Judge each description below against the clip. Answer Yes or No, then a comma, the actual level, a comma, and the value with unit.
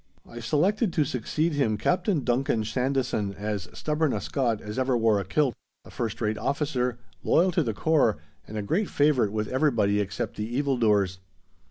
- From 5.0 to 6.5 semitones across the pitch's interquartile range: Yes, wide, 5.5 semitones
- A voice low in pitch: Yes, low, 125 Hz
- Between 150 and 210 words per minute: Yes, average, 180 wpm